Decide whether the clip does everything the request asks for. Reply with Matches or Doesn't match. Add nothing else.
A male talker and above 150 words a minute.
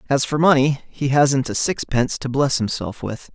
Matches